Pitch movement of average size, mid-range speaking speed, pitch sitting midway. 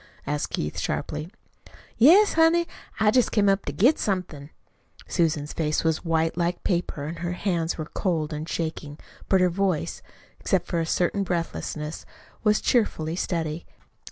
Yes: average, 4.0 semitones; average, 155 wpm; medium, 170 Hz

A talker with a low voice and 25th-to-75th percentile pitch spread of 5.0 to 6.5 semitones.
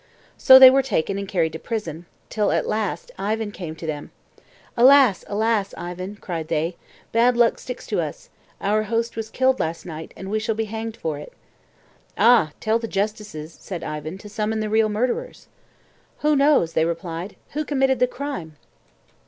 No: high, 210 Hz; wide, 5.6 semitones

